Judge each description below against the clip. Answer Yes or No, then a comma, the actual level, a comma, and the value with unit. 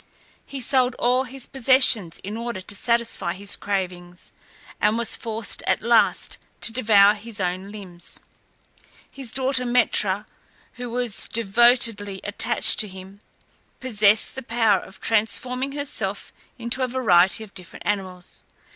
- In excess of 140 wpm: No, slow, 135 wpm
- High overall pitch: Yes, high, 220 Hz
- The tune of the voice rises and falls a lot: No, average, 3.9 semitones